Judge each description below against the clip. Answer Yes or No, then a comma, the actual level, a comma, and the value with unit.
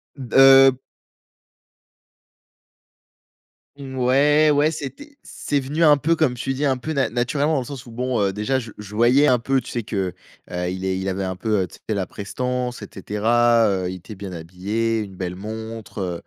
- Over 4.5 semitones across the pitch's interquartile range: Yes, average, 5.3 semitones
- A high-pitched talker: No, low, 120 Hz